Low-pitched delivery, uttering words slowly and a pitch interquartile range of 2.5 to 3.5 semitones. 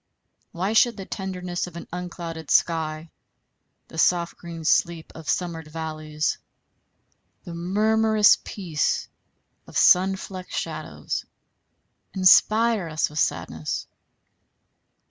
No: medium, 175 Hz; slow, 105 wpm; average, 2.9 semitones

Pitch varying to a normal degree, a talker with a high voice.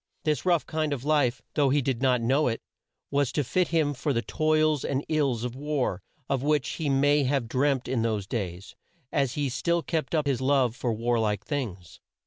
No: average, 3.7 semitones; low, 135 Hz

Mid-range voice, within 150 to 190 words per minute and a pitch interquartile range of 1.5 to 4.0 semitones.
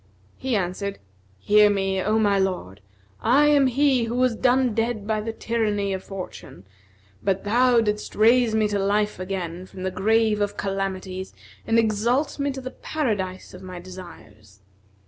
No: high, 210 Hz; average, 165 wpm; average, 3.6 semitones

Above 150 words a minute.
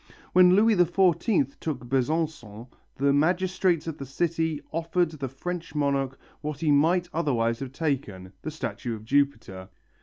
No: average, 145 wpm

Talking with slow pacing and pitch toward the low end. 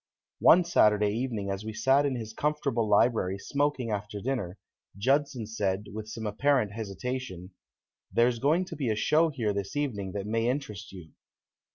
No: average, 165 wpm; low, 110 Hz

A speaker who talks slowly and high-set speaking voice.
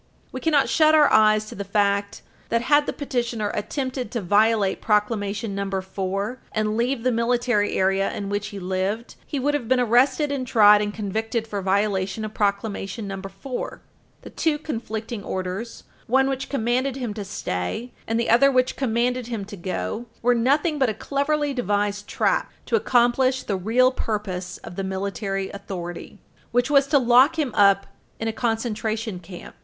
No: average, 175 wpm; high, 220 Hz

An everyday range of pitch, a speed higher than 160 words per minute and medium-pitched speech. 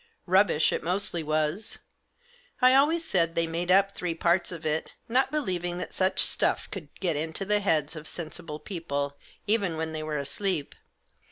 Yes: average, 4.0 semitones; average, 175 wpm; medium, 175 Hz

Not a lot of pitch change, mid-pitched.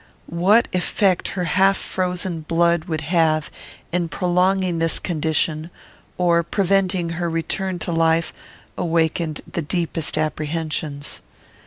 Yes: narrow, 2.0 semitones; medium, 170 Hz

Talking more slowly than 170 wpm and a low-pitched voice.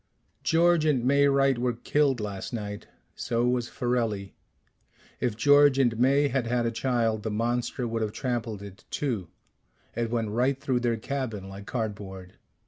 Yes: average, 160 wpm; low, 120 Hz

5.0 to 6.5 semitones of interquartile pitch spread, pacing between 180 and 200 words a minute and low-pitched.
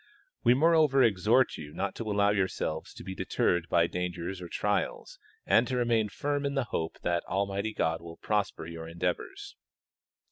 No: wide, 5.6 semitones; average, 170 wpm; low, 100 Hz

